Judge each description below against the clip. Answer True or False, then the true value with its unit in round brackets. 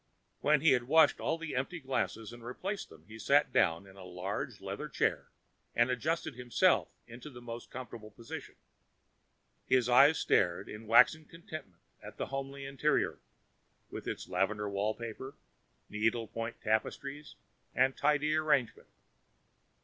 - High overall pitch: False (120 Hz)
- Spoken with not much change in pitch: False (5.0 semitones)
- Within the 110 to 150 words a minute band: True (140 wpm)